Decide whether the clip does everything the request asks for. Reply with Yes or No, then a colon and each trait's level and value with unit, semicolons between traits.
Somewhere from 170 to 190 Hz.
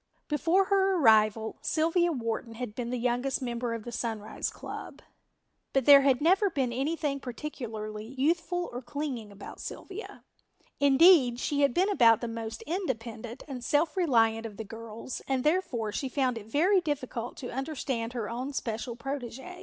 No: very high, 255 Hz